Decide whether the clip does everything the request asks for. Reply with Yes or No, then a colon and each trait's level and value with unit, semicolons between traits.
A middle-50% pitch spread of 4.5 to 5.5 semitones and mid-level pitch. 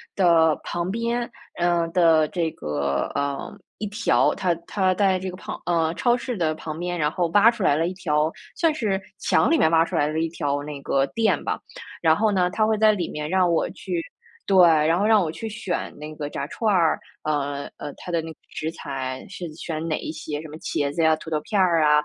No: average, 3.8 semitones; medium, 165 Hz